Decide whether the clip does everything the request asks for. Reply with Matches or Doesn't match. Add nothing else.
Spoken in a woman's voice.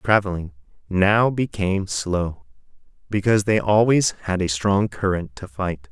Doesn't match